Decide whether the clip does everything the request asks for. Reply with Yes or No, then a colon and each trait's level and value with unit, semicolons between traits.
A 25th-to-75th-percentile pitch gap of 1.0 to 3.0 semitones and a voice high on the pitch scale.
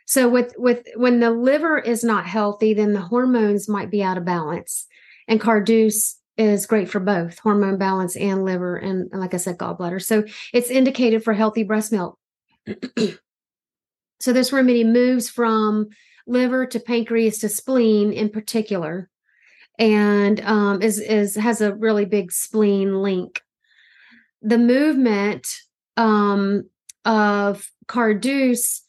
Yes: average, 2.7 semitones; high, 215 Hz